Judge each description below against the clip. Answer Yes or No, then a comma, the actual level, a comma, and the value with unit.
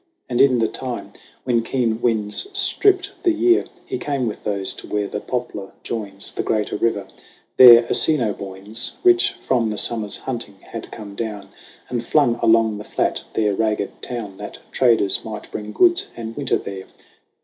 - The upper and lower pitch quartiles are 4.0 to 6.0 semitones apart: No, average, 3.5 semitones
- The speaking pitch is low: Yes, low, 115 Hz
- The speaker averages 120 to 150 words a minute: No, average, 165 wpm